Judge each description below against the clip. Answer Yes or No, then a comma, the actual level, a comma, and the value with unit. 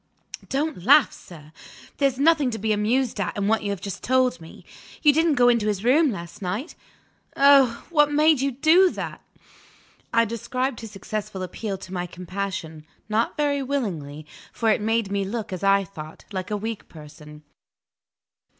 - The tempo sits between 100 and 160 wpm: No, average, 170 wpm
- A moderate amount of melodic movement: No, wide, 6.0 semitones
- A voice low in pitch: No, high, 220 Hz